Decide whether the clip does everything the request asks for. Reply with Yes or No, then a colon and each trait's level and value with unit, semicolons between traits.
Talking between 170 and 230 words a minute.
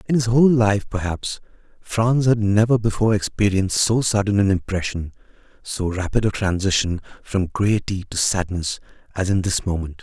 No: average, 155 wpm